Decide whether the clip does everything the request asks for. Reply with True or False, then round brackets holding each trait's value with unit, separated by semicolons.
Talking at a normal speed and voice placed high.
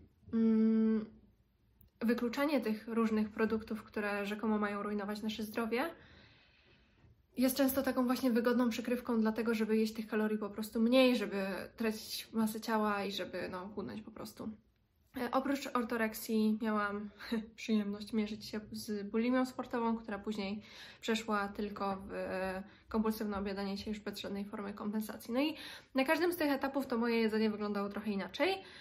True (145 wpm; 220 Hz)